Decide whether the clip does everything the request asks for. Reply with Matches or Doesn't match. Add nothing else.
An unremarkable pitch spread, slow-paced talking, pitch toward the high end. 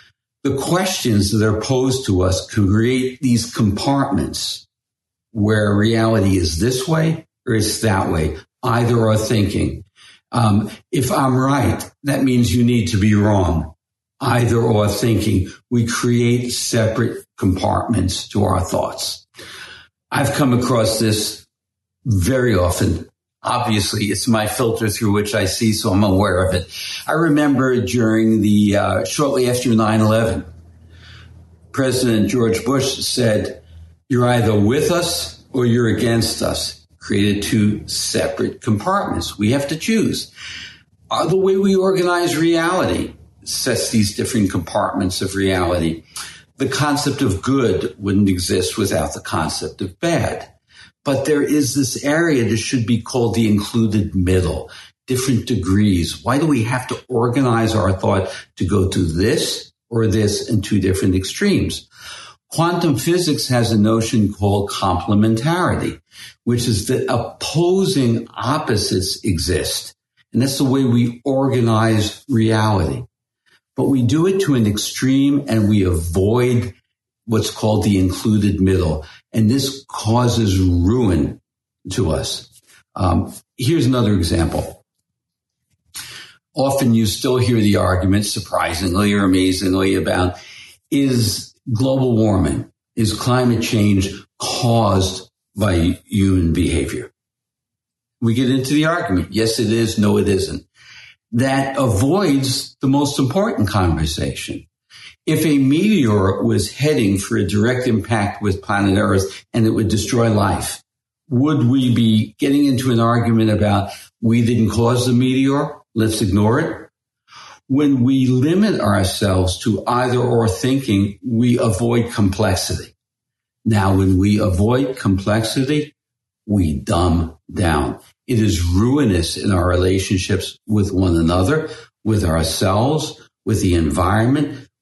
Doesn't match